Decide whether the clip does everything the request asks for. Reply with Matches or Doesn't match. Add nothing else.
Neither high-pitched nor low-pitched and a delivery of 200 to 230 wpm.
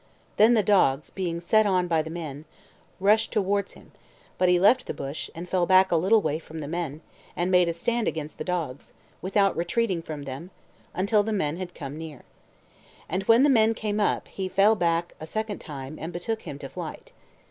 Matches